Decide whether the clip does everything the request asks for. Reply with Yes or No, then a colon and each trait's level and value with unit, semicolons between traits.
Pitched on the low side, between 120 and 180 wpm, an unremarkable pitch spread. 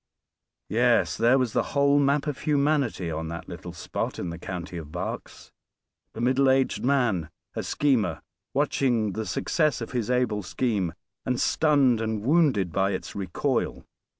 No: low, 120 Hz; average, 155 wpm; wide, 6.4 semitones